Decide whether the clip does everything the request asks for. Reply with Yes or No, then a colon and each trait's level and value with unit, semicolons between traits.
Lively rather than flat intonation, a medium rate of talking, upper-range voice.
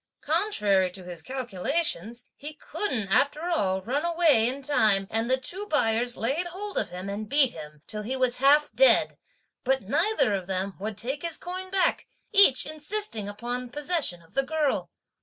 Yes: wide, 7.2 semitones; average, 175 wpm; very high, 255 Hz